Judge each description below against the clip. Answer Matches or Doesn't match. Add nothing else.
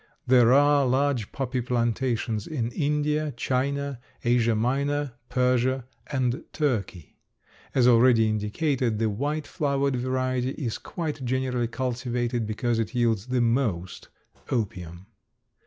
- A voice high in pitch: Doesn't match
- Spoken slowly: Matches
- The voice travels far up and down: Doesn't match